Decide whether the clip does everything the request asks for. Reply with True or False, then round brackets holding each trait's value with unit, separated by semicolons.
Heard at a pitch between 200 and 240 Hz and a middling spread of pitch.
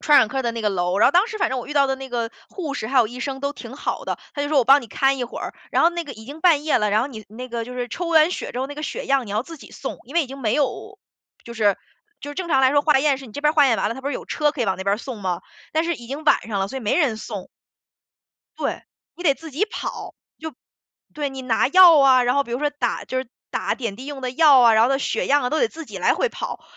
False (270 Hz; 3.9 semitones)